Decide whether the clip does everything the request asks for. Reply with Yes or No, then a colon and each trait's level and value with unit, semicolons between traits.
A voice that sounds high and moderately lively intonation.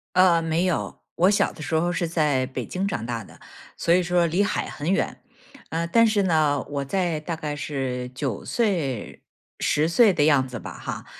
No: medium, 160 Hz; average, 4.0 semitones